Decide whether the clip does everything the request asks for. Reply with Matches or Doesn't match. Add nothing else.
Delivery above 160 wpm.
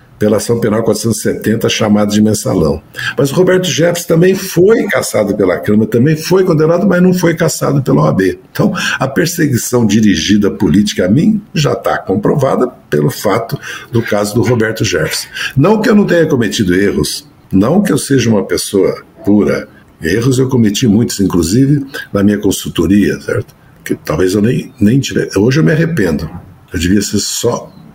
Matches